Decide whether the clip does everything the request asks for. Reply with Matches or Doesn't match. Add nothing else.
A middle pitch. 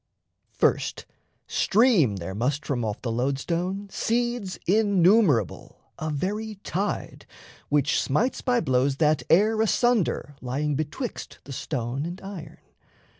Matches